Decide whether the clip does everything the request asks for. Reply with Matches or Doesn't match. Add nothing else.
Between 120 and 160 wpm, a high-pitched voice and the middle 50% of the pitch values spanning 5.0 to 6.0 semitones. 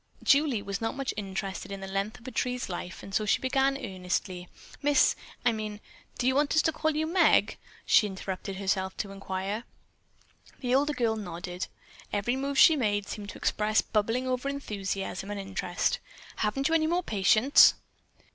Doesn't match